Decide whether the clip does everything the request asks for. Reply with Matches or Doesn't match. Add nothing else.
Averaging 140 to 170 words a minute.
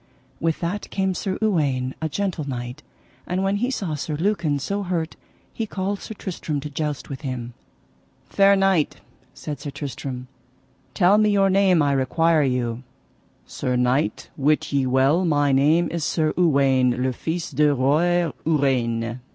Matches